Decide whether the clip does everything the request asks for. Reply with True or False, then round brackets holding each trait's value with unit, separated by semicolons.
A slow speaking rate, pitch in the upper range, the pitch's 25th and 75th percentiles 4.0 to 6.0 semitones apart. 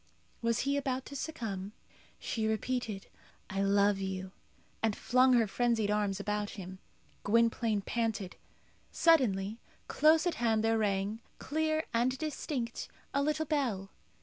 True (130 wpm; 225 Hz; 4.5 semitones)